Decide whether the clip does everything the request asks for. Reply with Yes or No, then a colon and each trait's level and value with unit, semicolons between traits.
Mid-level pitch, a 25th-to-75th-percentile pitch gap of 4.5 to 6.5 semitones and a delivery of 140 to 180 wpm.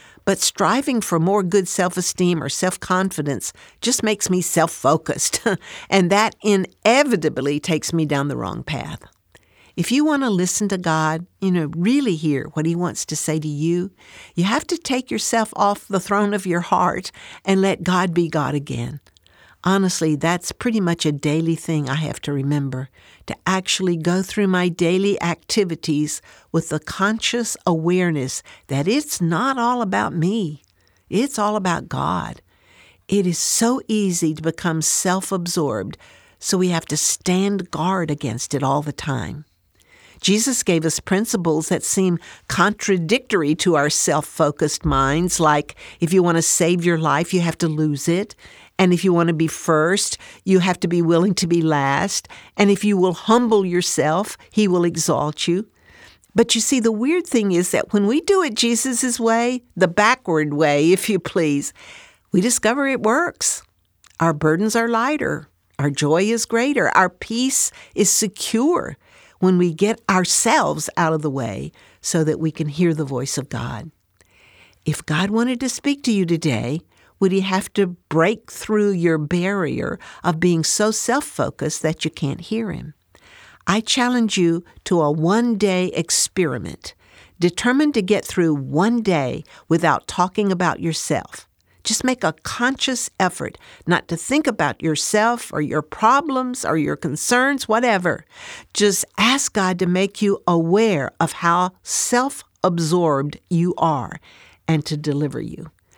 Yes: medium, 180 Hz; average, 5.1 semitones; average, 165 wpm